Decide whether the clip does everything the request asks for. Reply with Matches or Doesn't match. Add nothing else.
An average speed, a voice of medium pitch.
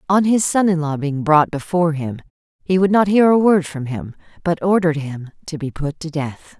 Doesn't match